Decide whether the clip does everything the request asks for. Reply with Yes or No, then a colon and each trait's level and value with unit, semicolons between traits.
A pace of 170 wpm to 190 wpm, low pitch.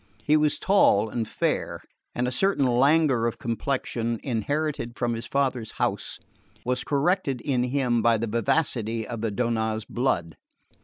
No: average, 150 wpm; low, 120 Hz